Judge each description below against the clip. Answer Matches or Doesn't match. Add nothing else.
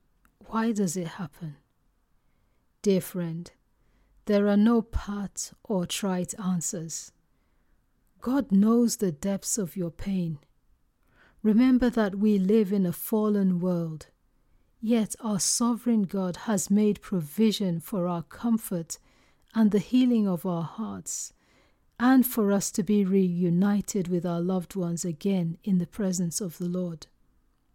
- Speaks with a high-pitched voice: Matches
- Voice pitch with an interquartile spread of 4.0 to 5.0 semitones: Doesn't match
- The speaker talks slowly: Matches